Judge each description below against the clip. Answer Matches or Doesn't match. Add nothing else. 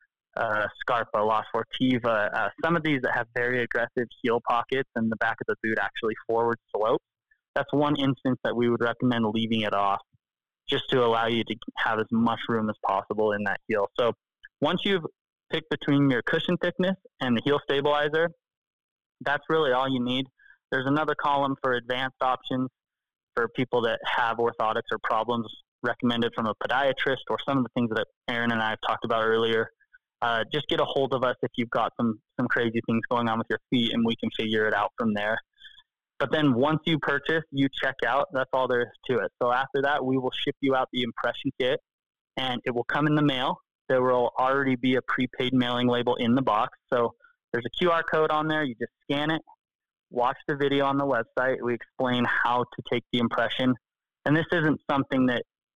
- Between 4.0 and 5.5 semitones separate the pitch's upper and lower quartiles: Doesn't match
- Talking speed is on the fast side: Matches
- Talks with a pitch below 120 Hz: Doesn't match